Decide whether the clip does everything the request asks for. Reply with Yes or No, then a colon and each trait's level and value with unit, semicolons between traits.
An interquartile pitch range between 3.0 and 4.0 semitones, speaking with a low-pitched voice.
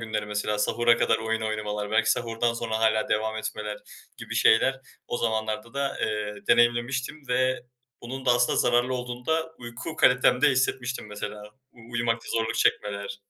No: narrow, 2.4 semitones; low, 115 Hz